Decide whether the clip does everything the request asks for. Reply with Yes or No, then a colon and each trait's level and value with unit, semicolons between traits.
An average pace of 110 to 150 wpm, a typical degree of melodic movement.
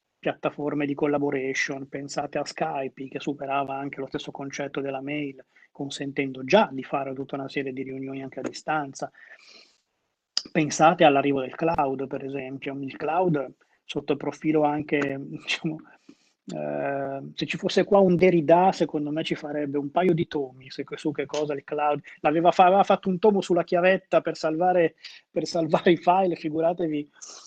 No: average, 160 wpm; average, 3.1 semitones